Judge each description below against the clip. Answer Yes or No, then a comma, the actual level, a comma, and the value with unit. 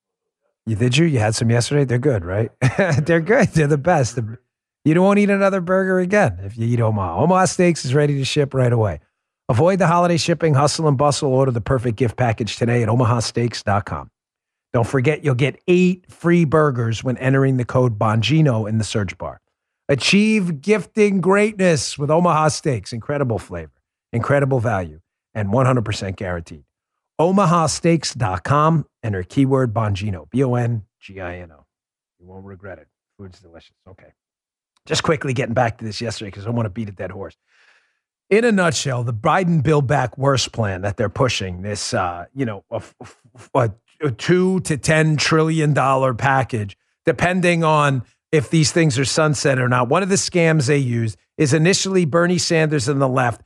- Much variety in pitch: Yes, wide, 5.9 semitones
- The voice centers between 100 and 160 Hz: Yes, low, 135 Hz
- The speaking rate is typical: Yes, average, 175 wpm